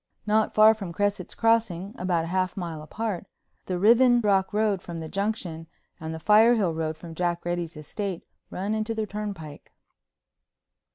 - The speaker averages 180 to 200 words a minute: No, average, 160 wpm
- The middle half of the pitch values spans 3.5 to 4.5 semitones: Yes, average, 4.0 semitones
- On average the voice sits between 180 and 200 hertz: Yes, high, 190 Hz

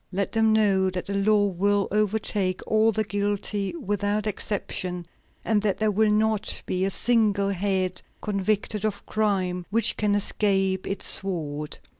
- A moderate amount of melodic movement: No, narrow, 1.9 semitones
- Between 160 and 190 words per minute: No, average, 150 wpm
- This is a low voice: No, high, 205 Hz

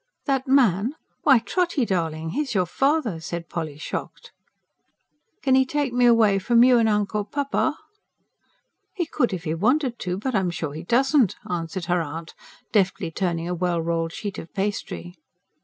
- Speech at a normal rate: Yes, average, 165 wpm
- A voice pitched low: No, high, 200 Hz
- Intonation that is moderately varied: No, wide, 7.2 semitones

